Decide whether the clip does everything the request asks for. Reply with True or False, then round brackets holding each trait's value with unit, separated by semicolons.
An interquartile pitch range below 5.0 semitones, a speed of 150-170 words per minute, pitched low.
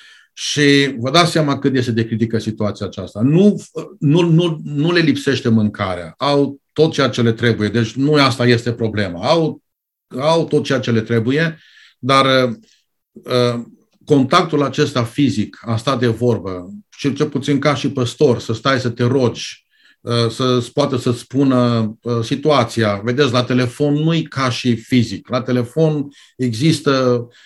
True (3.7 semitones; 160 wpm; 130 Hz)